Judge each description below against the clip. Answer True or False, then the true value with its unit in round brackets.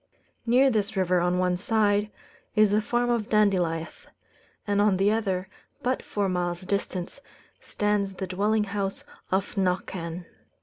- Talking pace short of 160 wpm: True (140 wpm)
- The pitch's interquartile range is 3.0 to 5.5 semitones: False (2.5 semitones)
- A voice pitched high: True (200 Hz)